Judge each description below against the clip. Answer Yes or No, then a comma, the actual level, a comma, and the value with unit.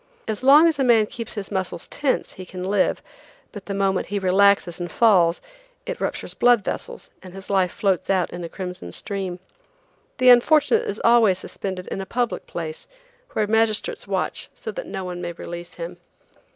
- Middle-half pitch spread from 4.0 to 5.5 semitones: Yes, average, 4.5 semitones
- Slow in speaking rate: No, average, 185 wpm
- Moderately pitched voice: No, high, 200 Hz